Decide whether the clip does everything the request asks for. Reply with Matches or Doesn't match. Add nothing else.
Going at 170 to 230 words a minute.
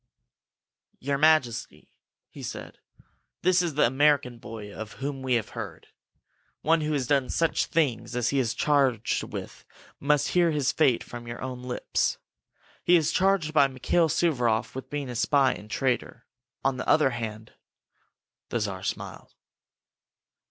Doesn't match